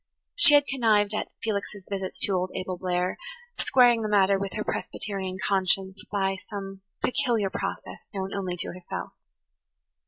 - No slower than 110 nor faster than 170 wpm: Yes, average, 150 wpm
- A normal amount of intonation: No, narrow, 2.2 semitones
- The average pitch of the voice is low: No, high, 195 Hz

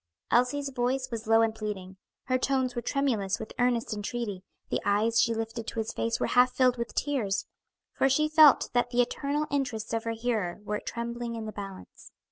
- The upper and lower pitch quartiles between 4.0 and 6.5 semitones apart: No, average, 2.7 semitones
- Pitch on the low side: No, high, 235 Hz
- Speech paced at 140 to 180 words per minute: No, average, 195 wpm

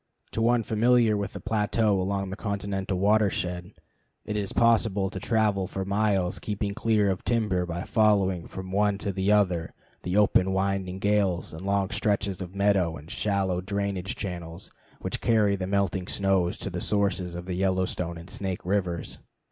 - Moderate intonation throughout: No, narrow, 2.1 semitones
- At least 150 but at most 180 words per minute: Yes, average, 170 wpm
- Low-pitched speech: Yes, low, 100 Hz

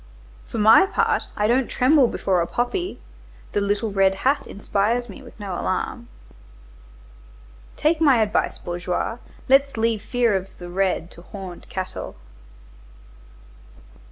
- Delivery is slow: Yes, slow, 130 wpm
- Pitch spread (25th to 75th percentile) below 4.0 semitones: No, average, 4.4 semitones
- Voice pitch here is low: No, high, 210 Hz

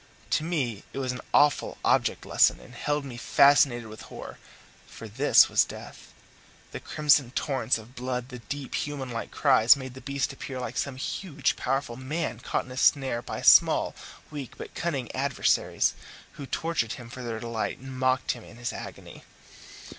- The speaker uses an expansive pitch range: No, average, 2.7 semitones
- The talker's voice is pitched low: Yes, low, 130 Hz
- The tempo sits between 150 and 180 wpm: Yes, average, 175 wpm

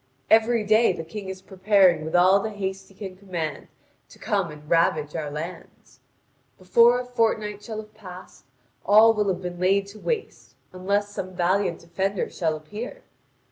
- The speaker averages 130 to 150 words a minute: No, average, 165 wpm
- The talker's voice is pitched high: Yes, high, 195 Hz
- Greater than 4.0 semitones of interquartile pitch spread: No, average, 3.2 semitones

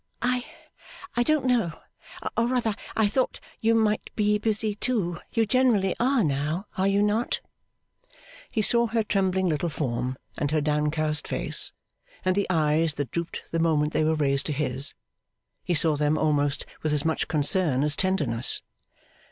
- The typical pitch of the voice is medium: Yes, medium, 170 Hz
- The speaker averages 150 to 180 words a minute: Yes, average, 160 wpm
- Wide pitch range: Yes, wide, 6.4 semitones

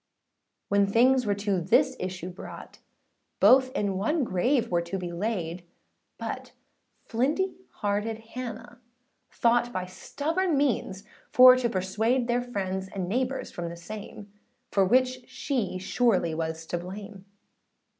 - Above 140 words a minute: No, slow, 135 wpm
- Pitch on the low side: No, high, 210 Hz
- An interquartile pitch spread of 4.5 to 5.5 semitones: Yes, average, 5.1 semitones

